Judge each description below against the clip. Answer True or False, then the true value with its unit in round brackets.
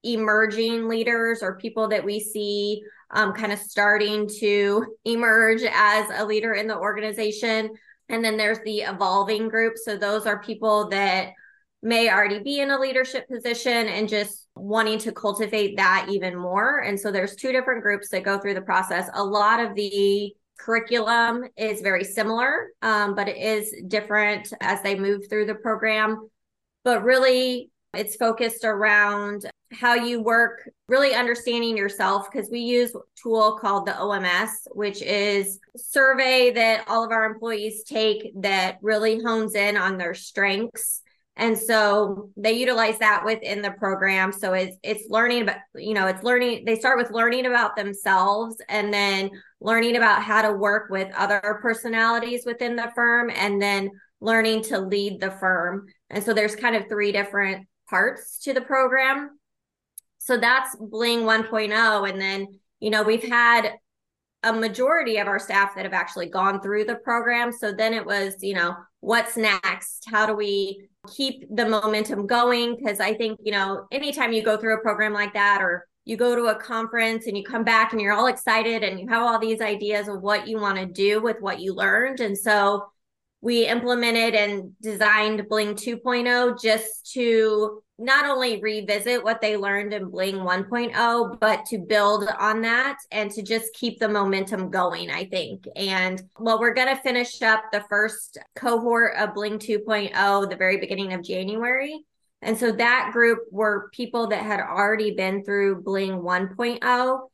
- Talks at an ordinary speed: True (175 wpm)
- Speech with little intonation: True (2.3 semitones)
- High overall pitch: True (215 Hz)